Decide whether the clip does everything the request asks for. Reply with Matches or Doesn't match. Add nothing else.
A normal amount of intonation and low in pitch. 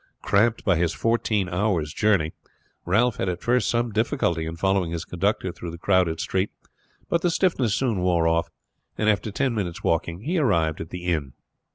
Matches